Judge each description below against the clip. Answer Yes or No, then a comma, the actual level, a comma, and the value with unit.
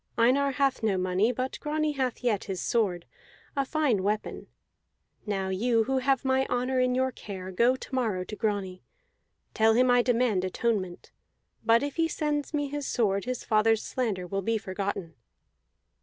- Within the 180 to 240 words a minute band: No, average, 170 wpm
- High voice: Yes, high, 230 Hz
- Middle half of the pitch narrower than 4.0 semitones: No, average, 4.8 semitones